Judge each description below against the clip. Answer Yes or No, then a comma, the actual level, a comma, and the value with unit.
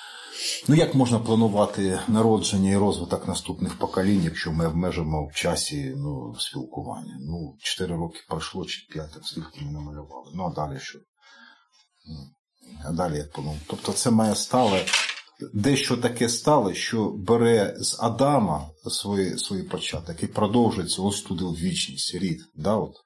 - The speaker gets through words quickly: No, average, 145 wpm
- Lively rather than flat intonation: Yes, wide, 6.8 semitones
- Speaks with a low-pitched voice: Yes, low, 100 Hz